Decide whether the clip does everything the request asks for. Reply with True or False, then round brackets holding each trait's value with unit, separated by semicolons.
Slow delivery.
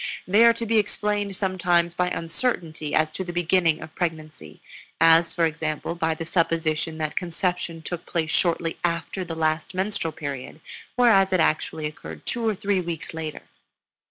False (165 wpm)